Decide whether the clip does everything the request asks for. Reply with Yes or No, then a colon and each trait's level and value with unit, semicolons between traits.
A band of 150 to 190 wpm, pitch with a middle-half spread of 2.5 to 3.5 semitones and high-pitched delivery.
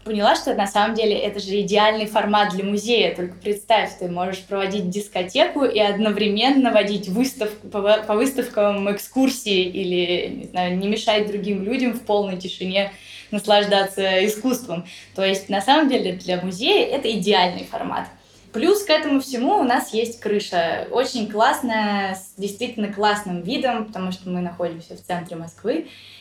Yes: average, 155 wpm; average, 2.9 semitones; high, 205 Hz